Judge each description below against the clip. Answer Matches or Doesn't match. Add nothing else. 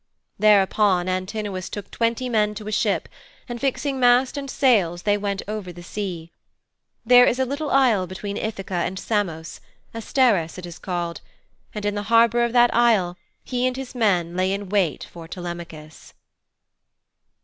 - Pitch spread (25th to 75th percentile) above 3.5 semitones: Matches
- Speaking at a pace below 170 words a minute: Matches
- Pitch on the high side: Matches